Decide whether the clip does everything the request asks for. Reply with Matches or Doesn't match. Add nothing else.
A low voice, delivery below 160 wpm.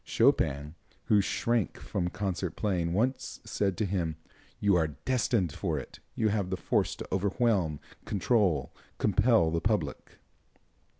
Matches